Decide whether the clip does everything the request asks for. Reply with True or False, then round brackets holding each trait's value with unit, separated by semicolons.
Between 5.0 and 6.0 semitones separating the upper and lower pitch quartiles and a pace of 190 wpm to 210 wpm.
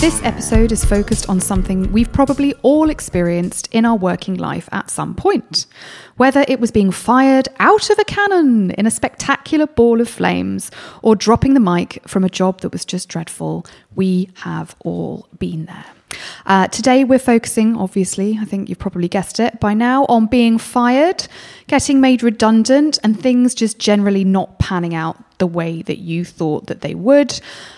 False (5.6 semitones; 175 wpm)